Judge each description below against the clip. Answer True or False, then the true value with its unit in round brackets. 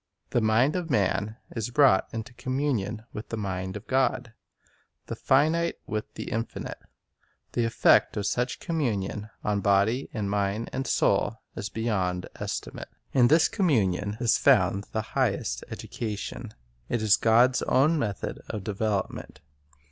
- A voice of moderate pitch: False (110 Hz)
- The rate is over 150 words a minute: False (145 wpm)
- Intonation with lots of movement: False (3.8 semitones)